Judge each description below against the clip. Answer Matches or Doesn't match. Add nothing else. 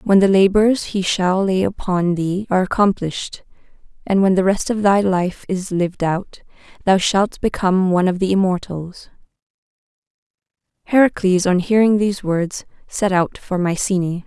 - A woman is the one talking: Matches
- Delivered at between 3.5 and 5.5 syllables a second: Matches